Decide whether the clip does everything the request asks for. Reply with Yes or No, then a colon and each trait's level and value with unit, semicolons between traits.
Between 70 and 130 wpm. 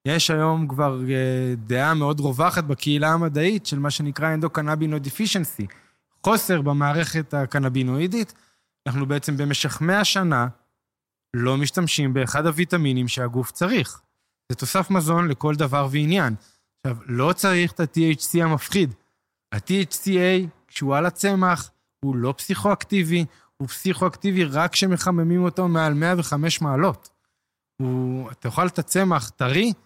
Yes: average, 125 wpm